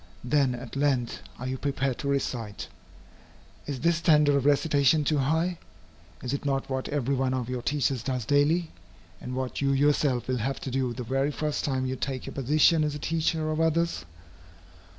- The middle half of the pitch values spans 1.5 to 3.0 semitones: Yes, narrow, 2.5 semitones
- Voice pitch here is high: No, medium, 140 Hz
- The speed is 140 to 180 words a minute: No, average, 190 wpm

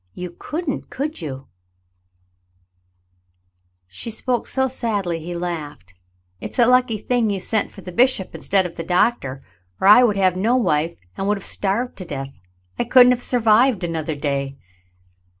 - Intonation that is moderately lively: No, wide, 6.4 semitones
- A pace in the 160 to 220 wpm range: Yes, average, 170 wpm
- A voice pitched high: Yes, high, 195 Hz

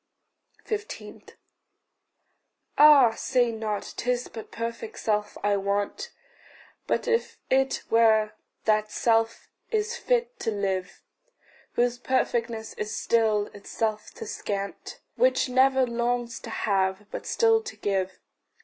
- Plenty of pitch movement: No, average, 4.0 semitones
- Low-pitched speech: No, high, 230 Hz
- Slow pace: Yes, slow, 115 wpm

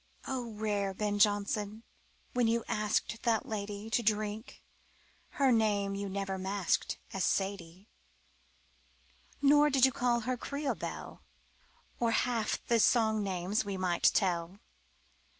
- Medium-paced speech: No, slow, 130 wpm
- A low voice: No, high, 210 Hz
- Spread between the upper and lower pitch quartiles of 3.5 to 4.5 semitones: No, average, 2.8 semitones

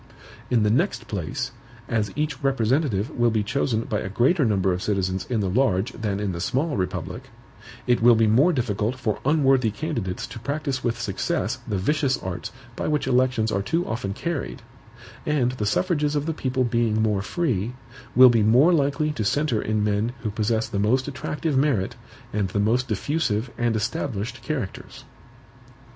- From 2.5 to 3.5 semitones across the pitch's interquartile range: No, average, 4.6 semitones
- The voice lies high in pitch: No, low, 120 Hz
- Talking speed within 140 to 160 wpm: No, average, 175 wpm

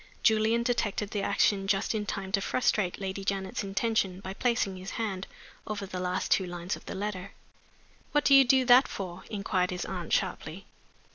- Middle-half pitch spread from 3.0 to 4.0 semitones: No, narrow, 2.6 semitones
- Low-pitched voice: No, high, 195 Hz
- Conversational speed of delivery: Yes, average, 185 wpm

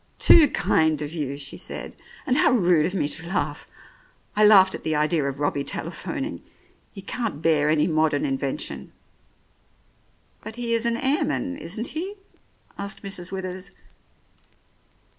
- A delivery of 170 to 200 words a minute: No, average, 155 wpm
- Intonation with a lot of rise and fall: Yes, wide, 6.8 semitones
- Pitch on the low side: No, medium, 180 Hz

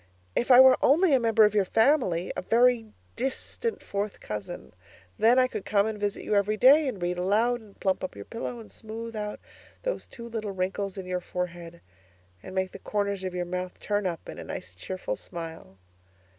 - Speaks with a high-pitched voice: Yes, high, 205 Hz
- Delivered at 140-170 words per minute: No, average, 200 wpm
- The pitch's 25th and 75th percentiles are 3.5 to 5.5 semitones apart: Yes, average, 4.2 semitones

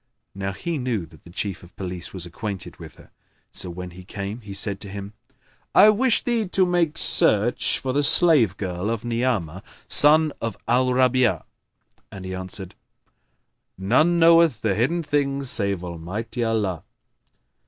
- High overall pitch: No, low, 110 Hz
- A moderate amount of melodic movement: No, wide, 6.7 semitones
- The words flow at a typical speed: Yes, average, 160 wpm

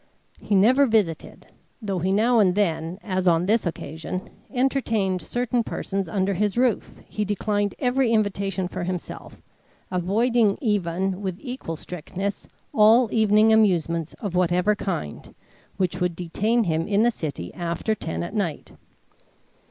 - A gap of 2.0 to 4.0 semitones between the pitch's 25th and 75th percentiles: Yes, average, 3.6 semitones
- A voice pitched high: Yes, high, 195 Hz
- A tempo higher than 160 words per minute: No, average, 140 wpm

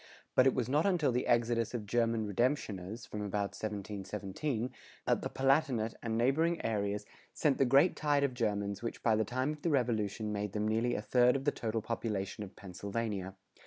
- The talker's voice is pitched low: Yes, low, 115 Hz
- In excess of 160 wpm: Yes, average, 190 wpm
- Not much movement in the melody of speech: No, average, 3.9 semitones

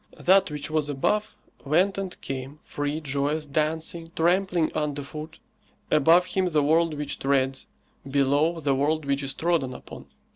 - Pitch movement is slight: No, average, 3.0 semitones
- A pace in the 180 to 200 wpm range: No, average, 150 wpm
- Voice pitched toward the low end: No, medium, 150 Hz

